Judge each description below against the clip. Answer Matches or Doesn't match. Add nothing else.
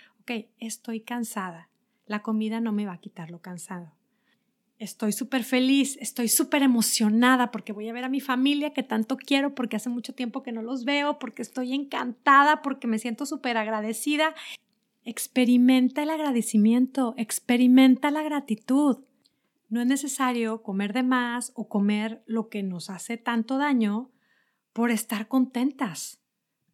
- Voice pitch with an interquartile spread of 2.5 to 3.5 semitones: Matches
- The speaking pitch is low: Doesn't match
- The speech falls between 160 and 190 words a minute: Doesn't match